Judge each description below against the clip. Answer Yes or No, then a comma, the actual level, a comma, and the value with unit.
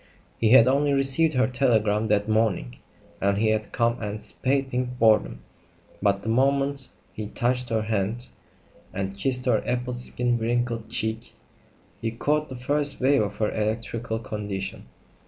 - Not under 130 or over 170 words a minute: Yes, average, 145 wpm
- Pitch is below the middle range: Yes, low, 115 Hz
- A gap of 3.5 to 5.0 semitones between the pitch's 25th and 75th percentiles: No, average, 3.1 semitones